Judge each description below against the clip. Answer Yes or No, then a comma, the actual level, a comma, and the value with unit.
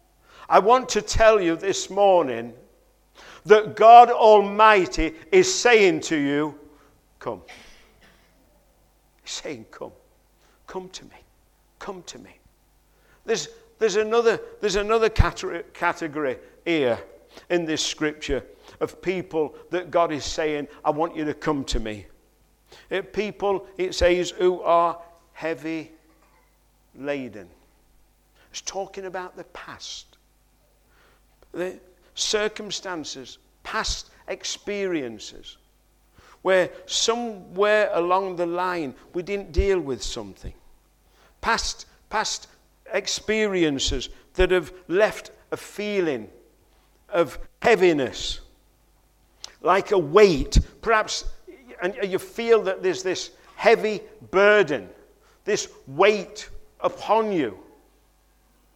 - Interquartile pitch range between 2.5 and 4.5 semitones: No, average, 4.9 semitones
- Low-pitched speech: No, medium, 185 Hz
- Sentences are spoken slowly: Yes, slow, 100 wpm